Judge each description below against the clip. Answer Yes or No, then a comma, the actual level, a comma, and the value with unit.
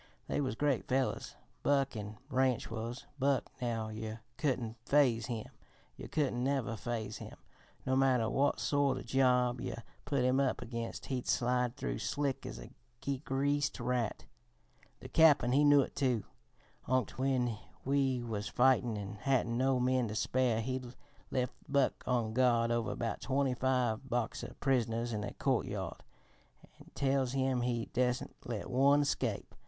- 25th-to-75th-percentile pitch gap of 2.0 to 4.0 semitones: Yes, narrow, 2.5 semitones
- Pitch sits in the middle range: No, low, 125 Hz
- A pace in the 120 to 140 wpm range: No, average, 155 wpm